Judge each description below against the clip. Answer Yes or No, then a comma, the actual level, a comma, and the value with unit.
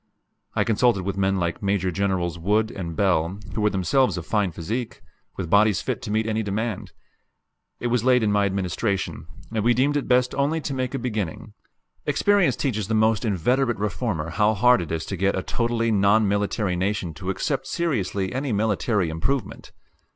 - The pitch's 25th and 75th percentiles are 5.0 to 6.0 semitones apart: No, average, 4.1 semitones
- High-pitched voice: No, low, 105 Hz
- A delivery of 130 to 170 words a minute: No, average, 185 wpm